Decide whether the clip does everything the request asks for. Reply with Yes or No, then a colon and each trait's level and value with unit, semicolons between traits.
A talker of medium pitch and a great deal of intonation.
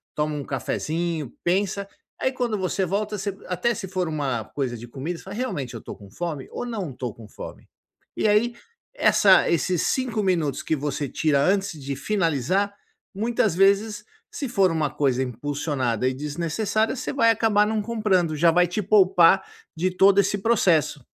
Yes: medium, 180 Hz; wide, 6.0 semitones